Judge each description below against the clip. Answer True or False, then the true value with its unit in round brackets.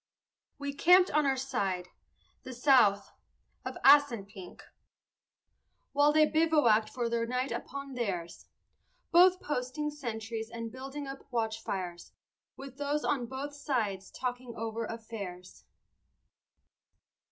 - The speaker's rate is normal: False (110 wpm)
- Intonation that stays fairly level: False (4.3 semitones)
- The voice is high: True (250 Hz)